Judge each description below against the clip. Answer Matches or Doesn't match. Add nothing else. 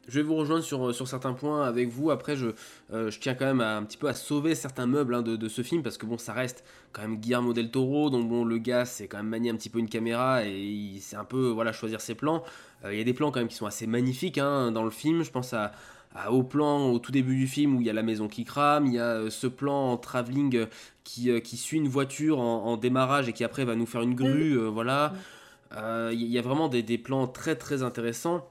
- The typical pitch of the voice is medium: Doesn't match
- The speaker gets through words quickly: Matches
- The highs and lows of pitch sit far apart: Doesn't match